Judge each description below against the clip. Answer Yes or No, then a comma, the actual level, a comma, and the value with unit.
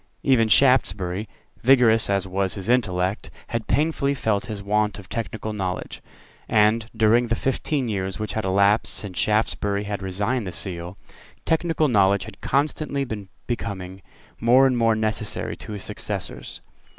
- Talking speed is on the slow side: No, average, 150 wpm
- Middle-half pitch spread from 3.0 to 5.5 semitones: Yes, average, 3.4 semitones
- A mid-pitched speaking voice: No, low, 105 Hz